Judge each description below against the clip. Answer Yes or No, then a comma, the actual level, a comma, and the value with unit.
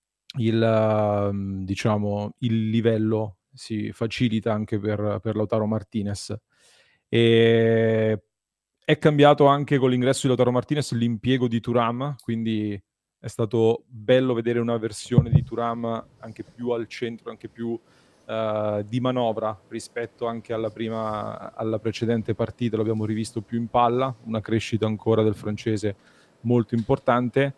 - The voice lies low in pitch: Yes, low, 115 Hz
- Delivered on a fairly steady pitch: Yes, narrow, 1.7 semitones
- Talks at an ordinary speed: Yes, average, 135 wpm